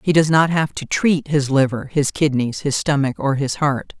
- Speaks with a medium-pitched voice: Yes, medium, 145 Hz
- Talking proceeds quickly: Yes, fast, 225 wpm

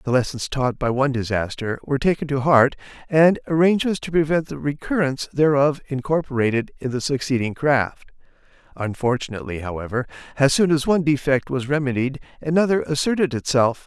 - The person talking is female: No, male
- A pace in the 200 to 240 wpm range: No, average, 145 wpm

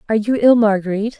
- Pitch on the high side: Yes, high, 220 Hz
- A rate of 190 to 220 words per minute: Yes, average, 200 wpm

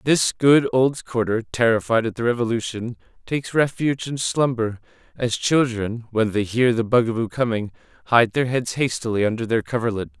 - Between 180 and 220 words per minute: No, average, 160 wpm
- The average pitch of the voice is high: No, low, 120 Hz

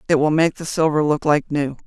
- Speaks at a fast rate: Yes, fast, 255 wpm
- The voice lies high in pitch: No, medium, 150 Hz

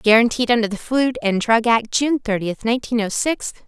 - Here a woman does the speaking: Yes, female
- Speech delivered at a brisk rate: No, average, 195 wpm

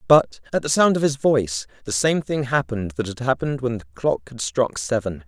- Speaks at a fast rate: Yes, fast, 230 wpm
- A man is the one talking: Yes, male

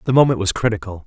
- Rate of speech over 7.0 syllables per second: Yes, 7.5 syllables/s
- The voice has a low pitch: Yes, low, 105 Hz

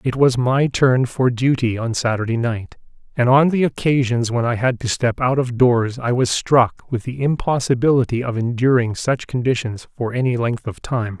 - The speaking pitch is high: No, low, 125 Hz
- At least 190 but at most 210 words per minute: Yes, average, 195 wpm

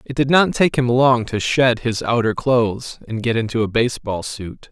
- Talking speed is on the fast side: Yes, fast, 215 wpm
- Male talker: Yes, male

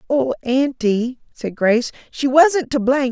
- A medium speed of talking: Yes, average, 155 wpm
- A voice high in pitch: Yes, very high, 255 Hz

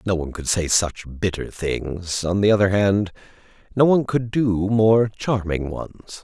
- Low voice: Yes, low, 100 Hz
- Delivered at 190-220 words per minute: No, average, 175 wpm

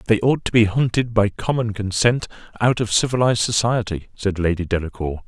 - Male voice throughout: Yes, male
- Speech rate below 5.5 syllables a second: No, 5.6 syllables/s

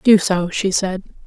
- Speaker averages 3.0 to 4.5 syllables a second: Yes, 3.9 syllables/s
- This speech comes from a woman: Yes, female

